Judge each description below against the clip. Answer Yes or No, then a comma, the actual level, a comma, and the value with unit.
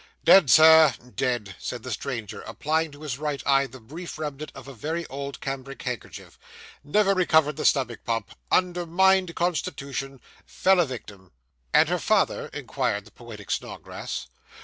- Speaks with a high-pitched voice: No, medium, 140 Hz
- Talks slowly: No, average, 150 wpm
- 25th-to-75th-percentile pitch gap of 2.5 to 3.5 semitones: No, average, 4.3 semitones